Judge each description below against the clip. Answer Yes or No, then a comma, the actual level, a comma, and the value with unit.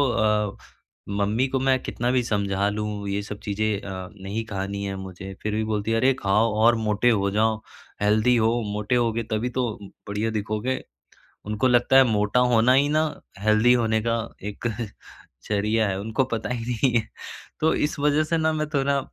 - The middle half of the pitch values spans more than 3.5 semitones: No, average, 3.2 semitones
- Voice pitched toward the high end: No, low, 110 Hz